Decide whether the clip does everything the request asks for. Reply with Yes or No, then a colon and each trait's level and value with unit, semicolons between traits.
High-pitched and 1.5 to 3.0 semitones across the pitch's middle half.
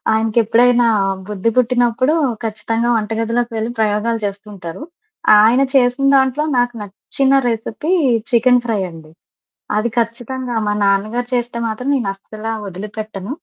Yes: high, 230 Hz; average, 2.7 semitones